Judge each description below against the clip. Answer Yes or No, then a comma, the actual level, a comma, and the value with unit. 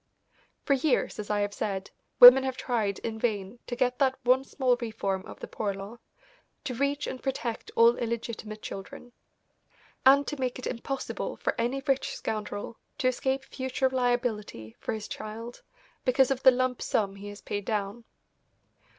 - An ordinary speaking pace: Yes, average, 170 wpm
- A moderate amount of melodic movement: Yes, average, 3.7 semitones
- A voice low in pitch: No, high, 240 Hz